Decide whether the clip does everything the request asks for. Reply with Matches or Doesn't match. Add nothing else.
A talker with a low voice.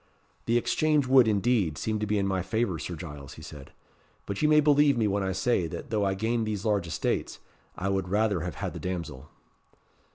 Matches